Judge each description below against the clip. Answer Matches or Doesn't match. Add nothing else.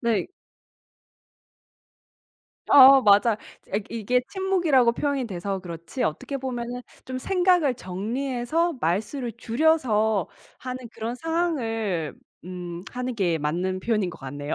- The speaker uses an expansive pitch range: Matches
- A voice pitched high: Matches